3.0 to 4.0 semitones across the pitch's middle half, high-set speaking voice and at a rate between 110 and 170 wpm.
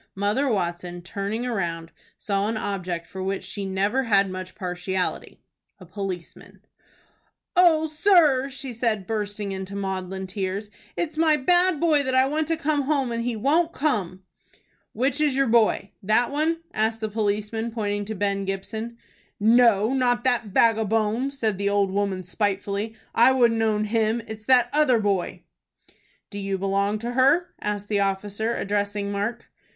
No: average, 4.5 semitones; high, 215 Hz; average, 155 wpm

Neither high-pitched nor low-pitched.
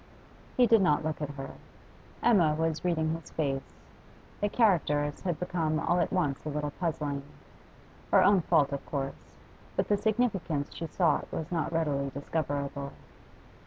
Yes: medium, 155 Hz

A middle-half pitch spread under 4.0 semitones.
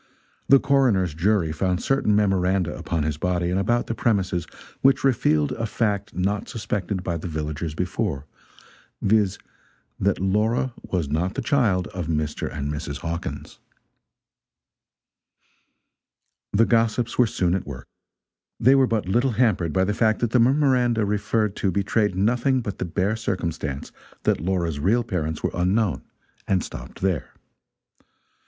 No: average, 4.8 semitones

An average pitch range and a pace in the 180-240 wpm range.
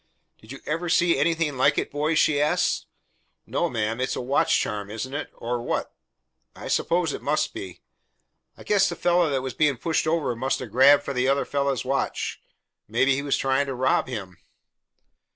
Yes: average, 3.4 semitones; average, 190 wpm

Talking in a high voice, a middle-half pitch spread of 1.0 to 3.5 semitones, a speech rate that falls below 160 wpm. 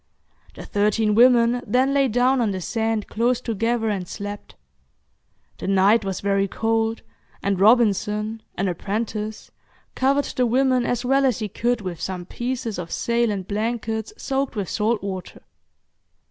Yes: high, 225 Hz; average, 3.2 semitones; average, 150 wpm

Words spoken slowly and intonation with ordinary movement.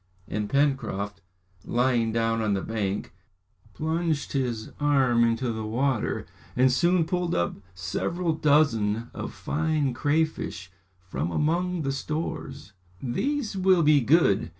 No: slow, 125 wpm; wide, 6.0 semitones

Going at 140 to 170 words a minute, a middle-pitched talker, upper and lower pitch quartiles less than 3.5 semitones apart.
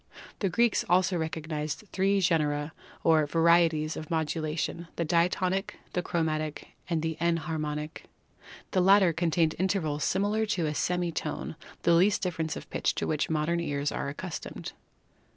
Yes: average, 155 wpm; medium, 165 Hz; narrow, 2.6 semitones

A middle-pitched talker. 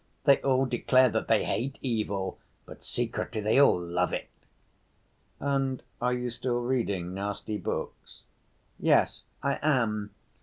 No: low, 120 Hz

